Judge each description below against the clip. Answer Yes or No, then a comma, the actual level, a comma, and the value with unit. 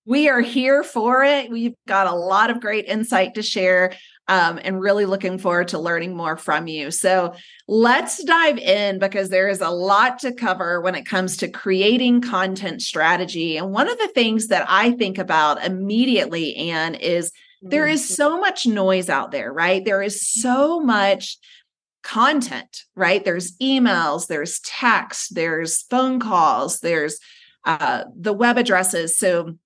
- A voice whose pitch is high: Yes, high, 195 Hz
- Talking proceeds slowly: No, average, 165 wpm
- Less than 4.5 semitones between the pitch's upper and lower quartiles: No, average, 5.2 semitones